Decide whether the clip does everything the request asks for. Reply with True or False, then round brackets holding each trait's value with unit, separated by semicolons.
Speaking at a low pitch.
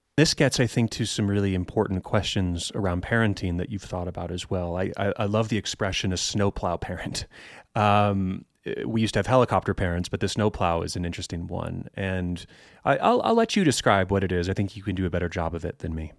True (100 Hz)